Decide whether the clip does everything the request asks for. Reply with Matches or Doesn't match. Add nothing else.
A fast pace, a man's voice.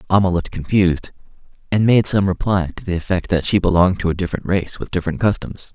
Matches